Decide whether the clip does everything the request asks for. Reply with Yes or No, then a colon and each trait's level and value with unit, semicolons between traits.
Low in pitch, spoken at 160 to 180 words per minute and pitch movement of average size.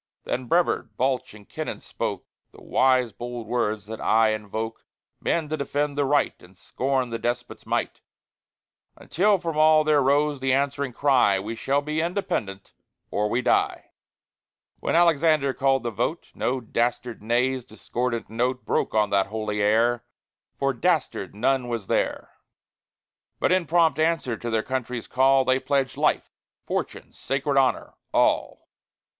No: low, 130 Hz; average, 150 wpm; average, 3.8 semitones